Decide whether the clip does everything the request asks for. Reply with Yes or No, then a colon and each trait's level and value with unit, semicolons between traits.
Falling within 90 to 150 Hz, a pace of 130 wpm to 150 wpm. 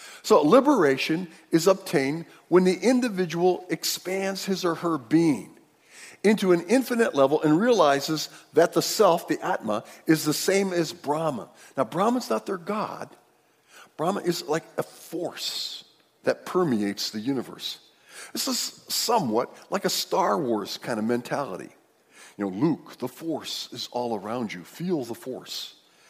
No: medium, 170 Hz; average, 145 wpm